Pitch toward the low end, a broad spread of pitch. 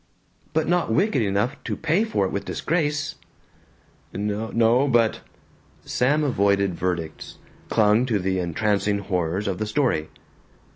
Yes: low, 105 Hz; wide, 6.1 semitones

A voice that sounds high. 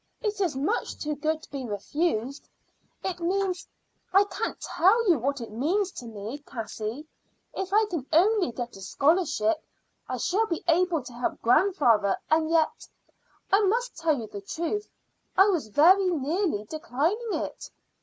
Yes: very high, 320 Hz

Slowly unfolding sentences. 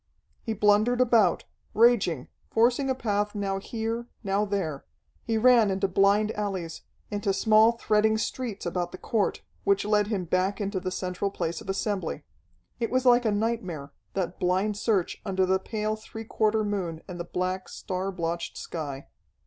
No: average, 165 wpm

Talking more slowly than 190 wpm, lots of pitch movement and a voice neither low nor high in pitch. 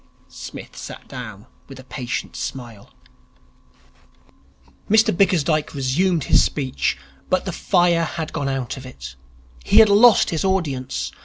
Yes: slow, 135 wpm; wide, 5.7 semitones; medium, 145 Hz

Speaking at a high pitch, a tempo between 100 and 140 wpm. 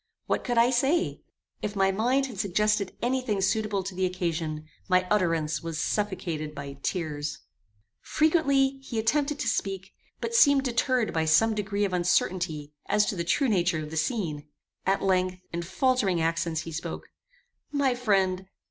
No: high, 195 Hz; average, 165 wpm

